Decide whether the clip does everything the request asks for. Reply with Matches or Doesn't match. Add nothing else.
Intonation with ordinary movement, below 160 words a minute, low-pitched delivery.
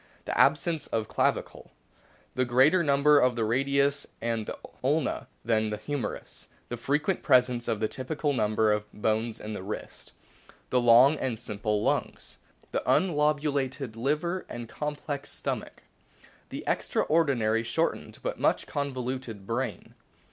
Matches